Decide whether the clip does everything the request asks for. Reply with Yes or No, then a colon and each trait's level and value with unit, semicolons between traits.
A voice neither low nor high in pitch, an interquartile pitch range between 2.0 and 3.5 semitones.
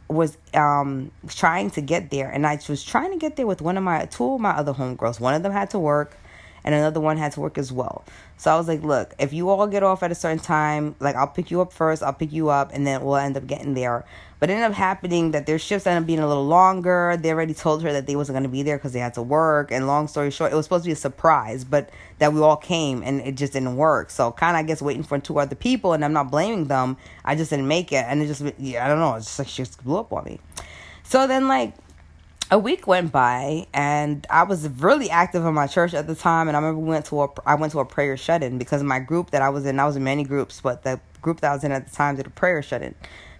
Yes: medium, 150 Hz; average, 3.2 semitones